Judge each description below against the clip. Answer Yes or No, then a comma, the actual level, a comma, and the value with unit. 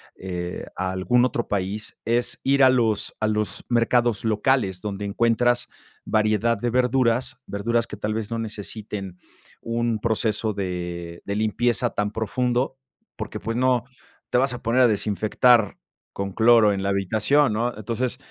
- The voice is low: Yes, low, 110 Hz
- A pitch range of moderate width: Yes, average, 3.0 semitones